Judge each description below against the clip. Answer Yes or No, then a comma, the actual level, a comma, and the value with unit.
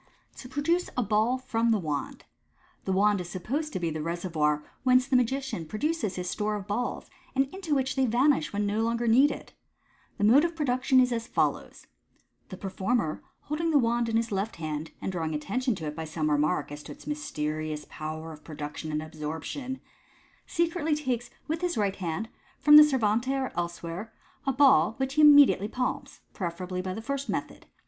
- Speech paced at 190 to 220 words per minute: Yes, average, 195 wpm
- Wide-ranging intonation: Yes, wide, 7.8 semitones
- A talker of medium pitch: No, high, 220 Hz